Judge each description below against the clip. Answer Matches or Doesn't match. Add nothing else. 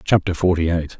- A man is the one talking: Matches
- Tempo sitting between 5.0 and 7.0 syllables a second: Matches